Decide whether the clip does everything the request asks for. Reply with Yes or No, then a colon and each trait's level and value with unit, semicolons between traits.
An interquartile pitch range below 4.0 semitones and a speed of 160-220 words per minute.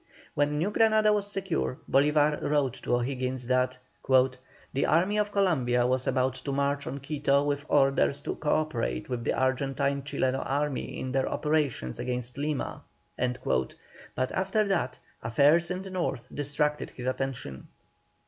No: average, 3.1 semitones; average, 150 wpm